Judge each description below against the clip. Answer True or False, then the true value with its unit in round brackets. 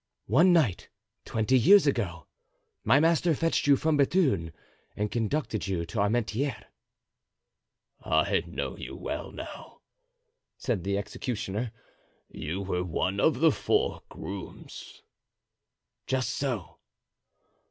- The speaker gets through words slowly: True (110 wpm)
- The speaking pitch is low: True (115 Hz)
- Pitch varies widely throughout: True (6.6 semitones)